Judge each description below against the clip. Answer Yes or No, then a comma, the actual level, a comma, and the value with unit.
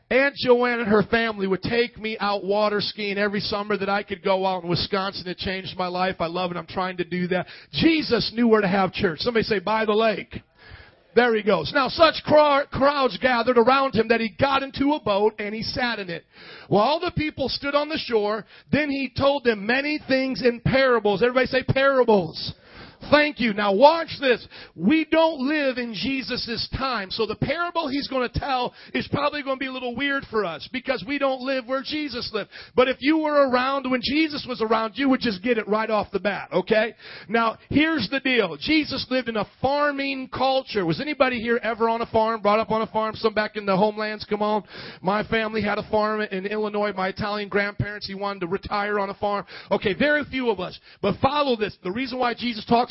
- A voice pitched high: Yes, high, 230 Hz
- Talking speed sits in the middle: No, fast, 220 wpm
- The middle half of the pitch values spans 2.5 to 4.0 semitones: No, average, 4.4 semitones